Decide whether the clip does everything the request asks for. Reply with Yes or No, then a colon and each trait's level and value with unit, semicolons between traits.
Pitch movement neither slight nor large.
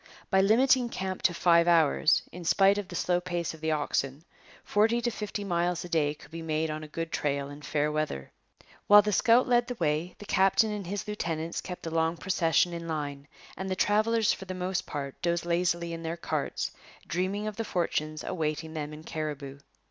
Yes: average, 3.9 semitones